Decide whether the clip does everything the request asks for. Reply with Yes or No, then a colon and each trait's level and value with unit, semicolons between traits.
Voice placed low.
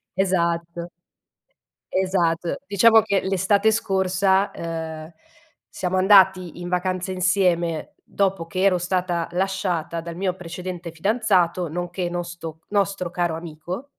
No: medium, 180 Hz